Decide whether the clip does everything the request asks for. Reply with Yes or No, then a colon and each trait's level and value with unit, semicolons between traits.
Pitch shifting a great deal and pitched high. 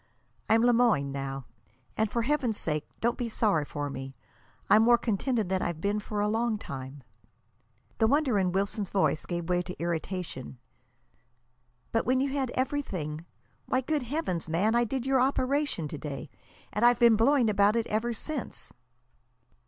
Yes: wide, 6.1 semitones; high, 215 Hz